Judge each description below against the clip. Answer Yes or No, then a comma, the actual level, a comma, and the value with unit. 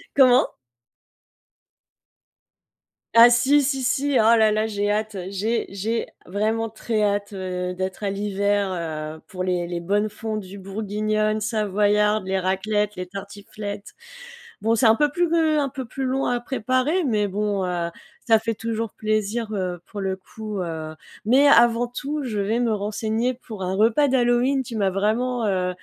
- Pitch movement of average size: Yes, average, 3.2 semitones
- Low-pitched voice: No, high, 215 Hz